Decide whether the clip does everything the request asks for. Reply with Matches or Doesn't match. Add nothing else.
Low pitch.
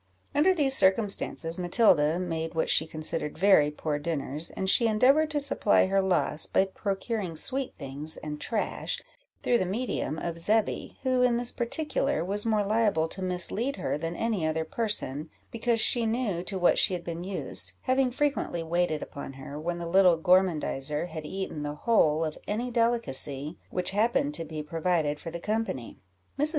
Doesn't match